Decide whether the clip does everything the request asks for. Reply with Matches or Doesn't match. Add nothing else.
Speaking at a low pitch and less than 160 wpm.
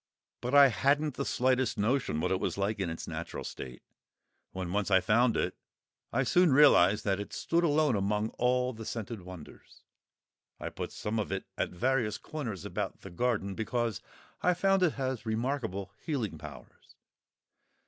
Doesn't match